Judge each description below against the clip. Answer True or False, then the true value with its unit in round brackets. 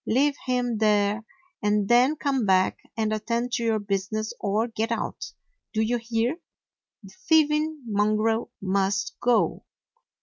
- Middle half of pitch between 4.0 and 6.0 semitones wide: False (2.9 semitones)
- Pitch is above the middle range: True (225 Hz)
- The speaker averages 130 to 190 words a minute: True (140 wpm)